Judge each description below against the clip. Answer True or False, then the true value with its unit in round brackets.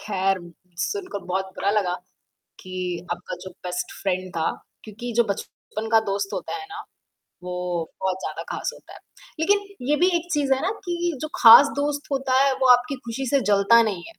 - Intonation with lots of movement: True (7.0 semitones)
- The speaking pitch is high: True (230 Hz)